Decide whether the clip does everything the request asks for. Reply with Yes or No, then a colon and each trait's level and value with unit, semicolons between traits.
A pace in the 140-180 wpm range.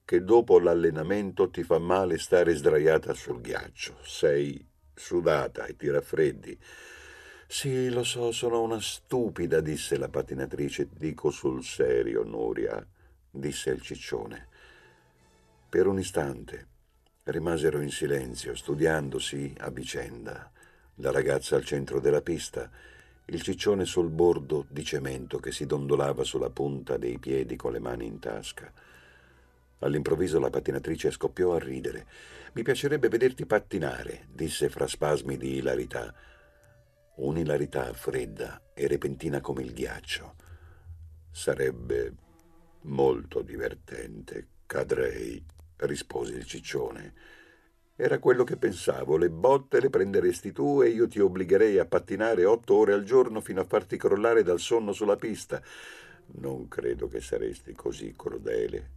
No: average, 130 wpm